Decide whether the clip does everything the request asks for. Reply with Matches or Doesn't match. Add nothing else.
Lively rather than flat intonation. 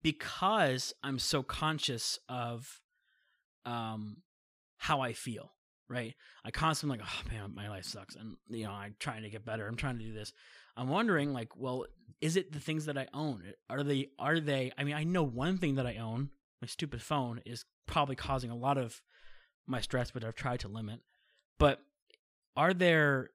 Doesn't match